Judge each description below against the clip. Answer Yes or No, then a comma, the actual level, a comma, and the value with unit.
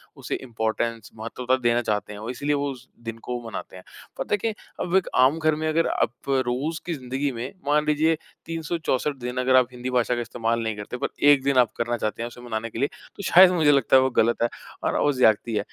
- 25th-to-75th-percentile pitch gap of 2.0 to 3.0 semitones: No, average, 4.1 semitones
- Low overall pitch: Yes, low, 125 Hz